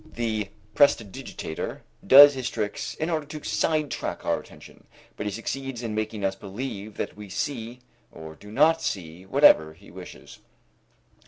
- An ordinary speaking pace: Yes, average, 150 wpm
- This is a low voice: Yes, low, 110 Hz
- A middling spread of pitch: No, wide, 5.7 semitones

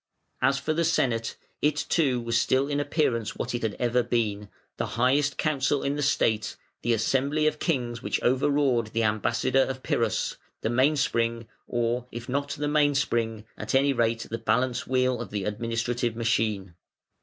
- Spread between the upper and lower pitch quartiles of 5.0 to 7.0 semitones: No, average, 3.3 semitones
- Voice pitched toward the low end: Yes, low, 120 Hz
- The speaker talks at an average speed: Yes, average, 175 wpm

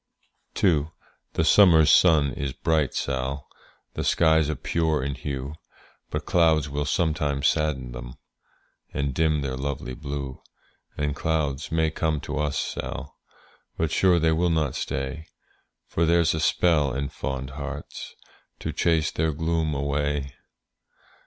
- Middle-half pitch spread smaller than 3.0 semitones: Yes, narrow, 2.5 semitones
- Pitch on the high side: No, very low, 75 Hz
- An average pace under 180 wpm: Yes, average, 140 wpm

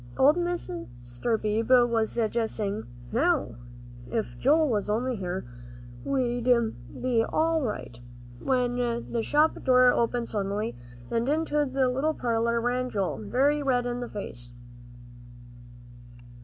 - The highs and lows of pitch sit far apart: No, average, 3.3 semitones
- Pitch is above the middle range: Yes, high, 240 Hz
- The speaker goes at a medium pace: No, slow, 125 wpm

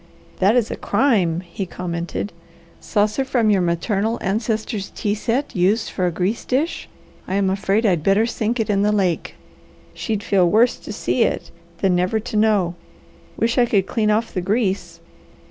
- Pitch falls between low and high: No, high, 205 Hz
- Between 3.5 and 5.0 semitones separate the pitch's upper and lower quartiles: No, average, 3.1 semitones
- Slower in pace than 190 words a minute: Yes, average, 175 wpm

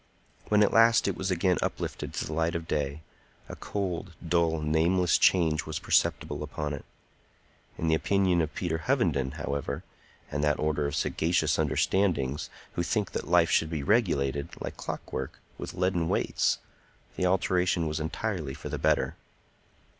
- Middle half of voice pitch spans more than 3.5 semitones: No, average, 3.2 semitones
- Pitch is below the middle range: Yes, very low, 80 Hz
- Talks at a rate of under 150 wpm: No, average, 160 wpm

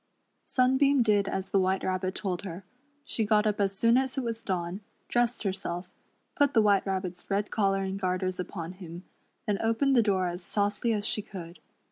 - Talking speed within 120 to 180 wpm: No, average, 190 wpm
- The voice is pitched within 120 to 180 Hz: No, high, 200 Hz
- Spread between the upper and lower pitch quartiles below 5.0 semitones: Yes, average, 3.3 semitones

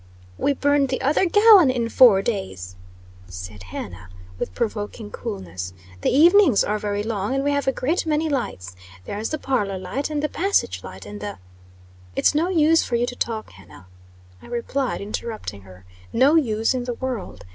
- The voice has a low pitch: No, high, 230 Hz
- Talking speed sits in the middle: Yes, average, 180 wpm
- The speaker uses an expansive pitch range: Yes, wide, 7.8 semitones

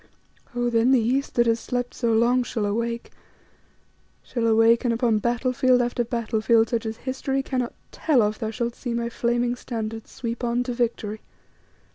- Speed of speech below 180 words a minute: Yes, average, 170 wpm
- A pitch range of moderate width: No, narrow, 1.4 semitones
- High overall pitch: Yes, high, 235 Hz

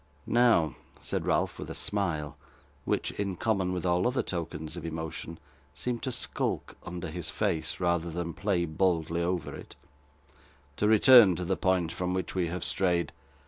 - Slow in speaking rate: No, average, 165 wpm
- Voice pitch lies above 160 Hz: No, very low, 90 Hz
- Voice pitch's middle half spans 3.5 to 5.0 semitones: No, narrow, 2.4 semitones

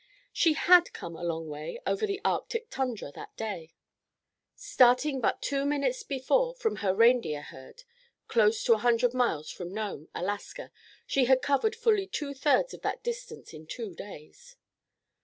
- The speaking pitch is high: Yes, very high, 255 Hz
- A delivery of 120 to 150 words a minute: No, average, 160 wpm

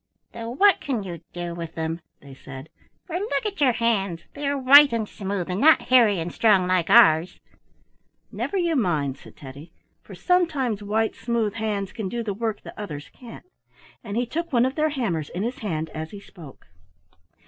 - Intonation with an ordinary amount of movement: No, wide, 6.8 semitones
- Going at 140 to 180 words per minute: No, average, 190 wpm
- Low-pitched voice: No, high, 215 Hz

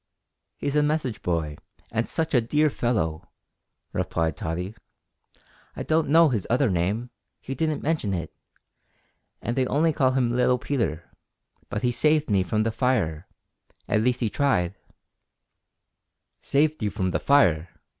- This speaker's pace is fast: No, average, 150 wpm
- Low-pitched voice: Yes, low, 120 Hz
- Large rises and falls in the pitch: Yes, wide, 7.4 semitones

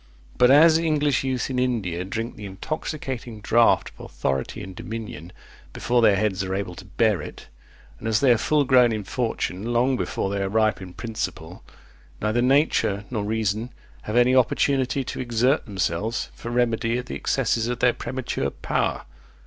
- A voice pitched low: Yes, low, 115 Hz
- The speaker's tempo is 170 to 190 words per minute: Yes, average, 175 wpm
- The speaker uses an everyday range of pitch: Yes, average, 3.7 semitones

